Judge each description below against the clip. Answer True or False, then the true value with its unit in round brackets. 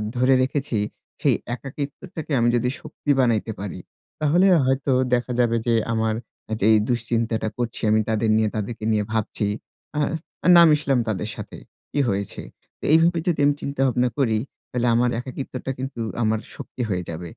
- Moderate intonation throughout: True (3.6 semitones)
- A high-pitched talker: False (120 Hz)